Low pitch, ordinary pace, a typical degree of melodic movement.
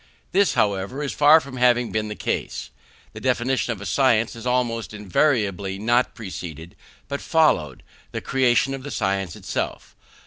Yes: low, 120 Hz; average, 160 wpm; average, 5.0 semitones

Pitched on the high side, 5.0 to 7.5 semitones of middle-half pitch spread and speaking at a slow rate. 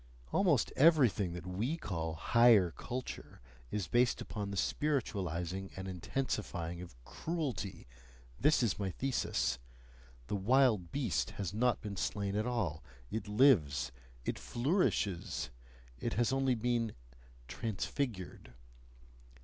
No: low, 105 Hz; wide, 5.5 semitones; slow, 115 wpm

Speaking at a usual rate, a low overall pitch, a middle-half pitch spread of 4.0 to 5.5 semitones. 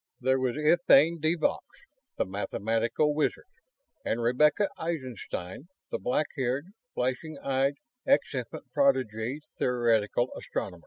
No: slow, 115 wpm; low, 130 Hz; average, 4.6 semitones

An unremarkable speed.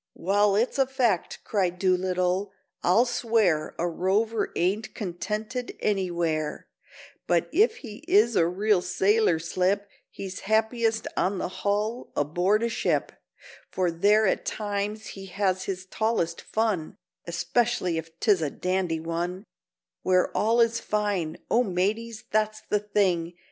No: slow, 130 wpm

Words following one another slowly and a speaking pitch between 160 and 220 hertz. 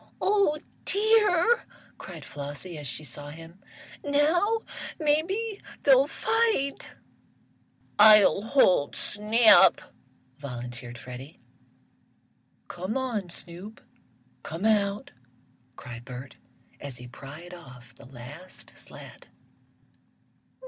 Yes: slow, 90 wpm; medium, 185 Hz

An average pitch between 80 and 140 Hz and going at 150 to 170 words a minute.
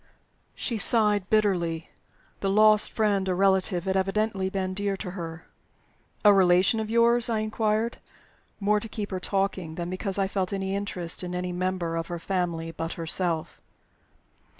No: high, 190 Hz; average, 160 wpm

